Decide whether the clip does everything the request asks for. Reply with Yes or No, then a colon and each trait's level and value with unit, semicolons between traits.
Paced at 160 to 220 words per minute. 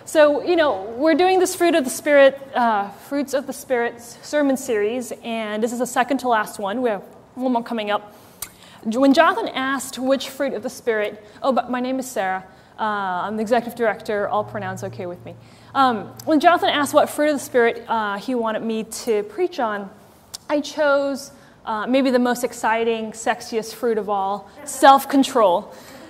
Yes: average, 190 wpm